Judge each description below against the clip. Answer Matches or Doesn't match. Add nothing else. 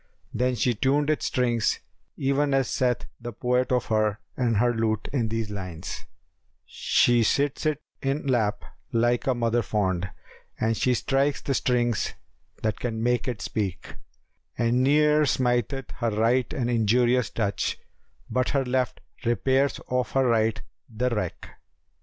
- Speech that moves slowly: Doesn't match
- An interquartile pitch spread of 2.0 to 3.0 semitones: Matches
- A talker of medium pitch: Doesn't match